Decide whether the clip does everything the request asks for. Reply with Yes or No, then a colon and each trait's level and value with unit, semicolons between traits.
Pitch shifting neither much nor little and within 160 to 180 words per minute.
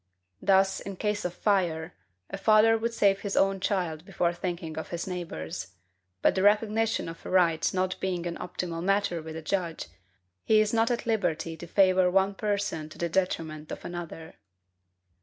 Yes: average, 3.4 semitones; average, 175 wpm